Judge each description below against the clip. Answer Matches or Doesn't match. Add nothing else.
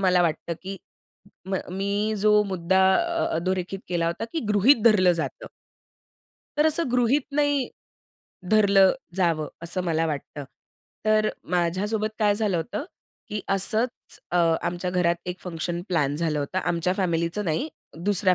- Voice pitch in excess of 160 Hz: Matches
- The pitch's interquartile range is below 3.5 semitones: Doesn't match